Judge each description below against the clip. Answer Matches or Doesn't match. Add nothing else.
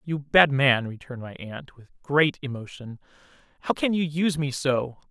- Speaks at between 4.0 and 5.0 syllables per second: Matches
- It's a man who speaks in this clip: Matches